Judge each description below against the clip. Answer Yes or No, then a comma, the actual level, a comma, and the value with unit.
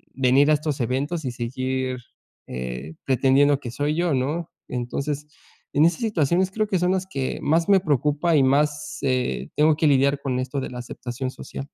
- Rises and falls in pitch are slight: No, average, 3.4 semitones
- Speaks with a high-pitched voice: No, medium, 140 Hz